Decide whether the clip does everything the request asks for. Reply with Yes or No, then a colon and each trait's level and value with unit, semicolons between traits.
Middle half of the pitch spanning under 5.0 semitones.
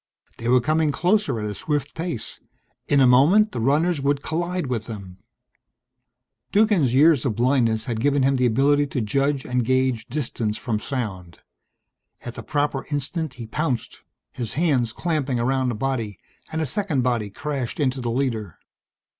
Yes: average, 3.9 semitones